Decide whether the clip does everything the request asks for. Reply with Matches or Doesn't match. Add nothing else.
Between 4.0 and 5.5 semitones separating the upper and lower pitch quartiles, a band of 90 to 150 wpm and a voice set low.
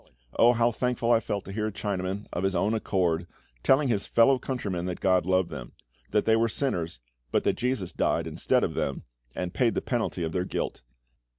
Doesn't match